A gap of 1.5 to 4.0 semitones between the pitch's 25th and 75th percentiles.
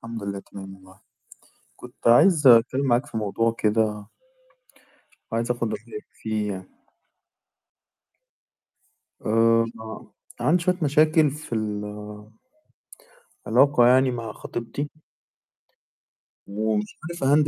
No: average, 4.5 semitones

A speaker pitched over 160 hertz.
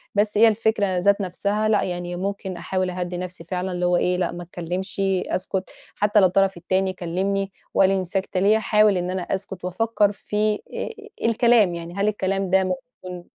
Yes: high, 190 Hz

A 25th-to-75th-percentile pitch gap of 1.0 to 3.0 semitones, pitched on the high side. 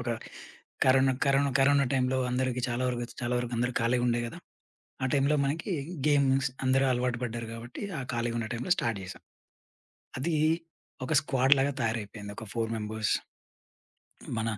No: narrow, 2.5 semitones; low, 125 Hz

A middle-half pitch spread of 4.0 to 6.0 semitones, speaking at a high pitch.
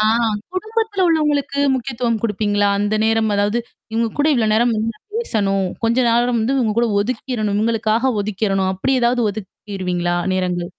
No: average, 3.2 semitones; high, 225 Hz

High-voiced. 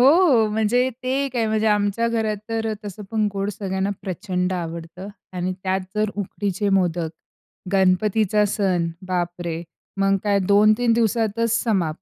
Yes: high, 205 Hz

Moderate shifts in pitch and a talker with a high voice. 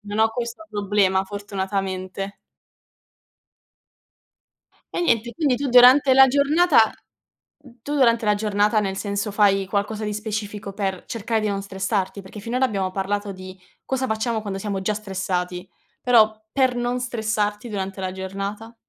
Yes: average, 3.1 semitones; high, 210 Hz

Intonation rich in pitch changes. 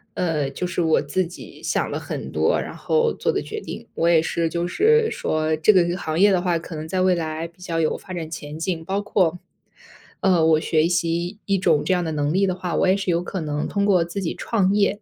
No: average, 2.9 semitones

